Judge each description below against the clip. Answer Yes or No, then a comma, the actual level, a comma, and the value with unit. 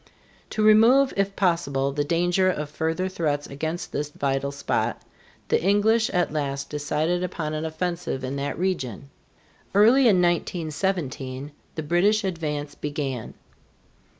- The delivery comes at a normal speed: No, slow, 130 wpm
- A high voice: No, medium, 160 Hz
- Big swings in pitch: No, average, 4.4 semitones